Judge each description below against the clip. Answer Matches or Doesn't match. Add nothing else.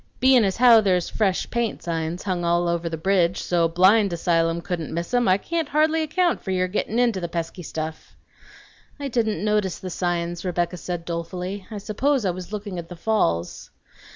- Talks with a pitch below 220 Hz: Matches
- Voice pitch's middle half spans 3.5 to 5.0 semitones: Matches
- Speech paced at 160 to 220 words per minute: Matches